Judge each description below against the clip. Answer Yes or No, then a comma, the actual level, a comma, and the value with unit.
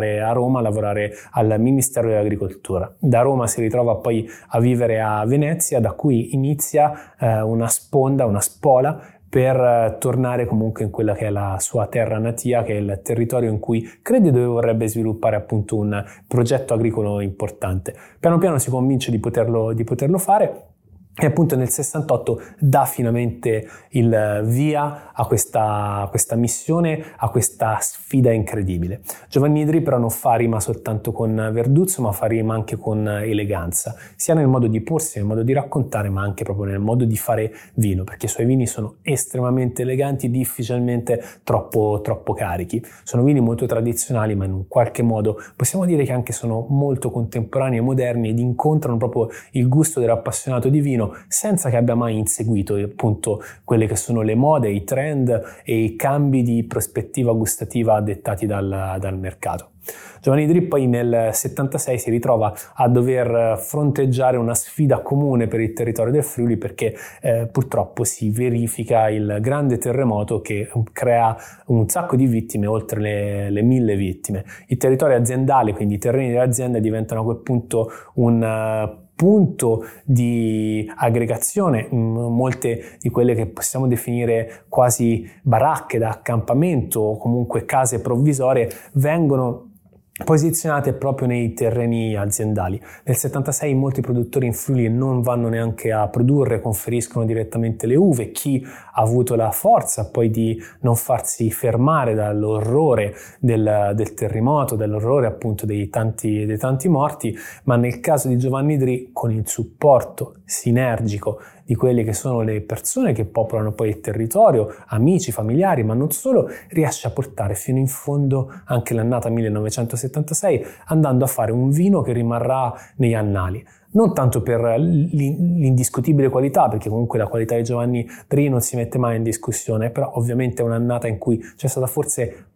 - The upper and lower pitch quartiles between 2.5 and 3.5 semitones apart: Yes, average, 2.9 semitones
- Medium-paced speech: Yes, average, 155 wpm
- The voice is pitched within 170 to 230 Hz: No, low, 120 Hz